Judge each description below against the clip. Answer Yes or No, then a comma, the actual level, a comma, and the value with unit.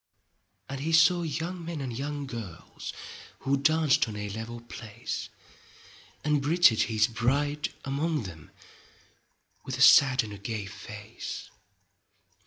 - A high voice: No, low, 135 Hz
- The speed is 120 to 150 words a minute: Yes, slow, 135 wpm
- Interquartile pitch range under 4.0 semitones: No, average, 5.0 semitones